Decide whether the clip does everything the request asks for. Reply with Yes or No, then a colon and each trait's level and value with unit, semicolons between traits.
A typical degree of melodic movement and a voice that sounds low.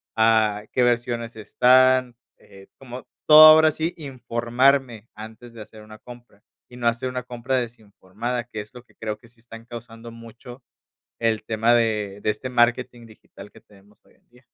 No: narrow, 2.1 semitones; low, 120 Hz